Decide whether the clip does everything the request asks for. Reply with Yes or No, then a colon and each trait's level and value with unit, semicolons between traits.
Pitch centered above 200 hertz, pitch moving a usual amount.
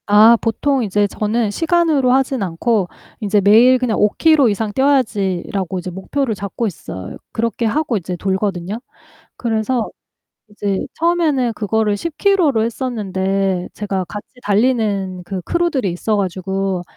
Yes: high, 215 Hz; average, 4.8 semitones